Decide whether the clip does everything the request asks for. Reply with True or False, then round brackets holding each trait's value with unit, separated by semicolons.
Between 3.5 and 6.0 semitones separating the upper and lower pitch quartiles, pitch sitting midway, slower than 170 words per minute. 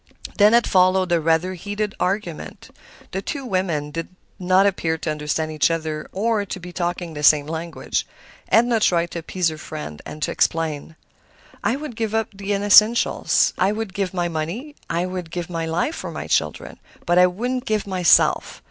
False (4.0 semitones; 180 Hz; 180 wpm)